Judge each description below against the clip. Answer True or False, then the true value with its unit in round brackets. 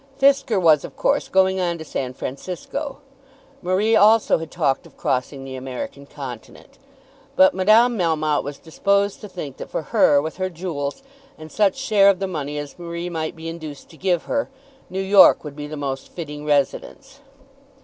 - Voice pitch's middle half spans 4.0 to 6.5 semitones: True (4.9 semitones)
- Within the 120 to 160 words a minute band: False (180 wpm)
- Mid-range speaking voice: True (170 Hz)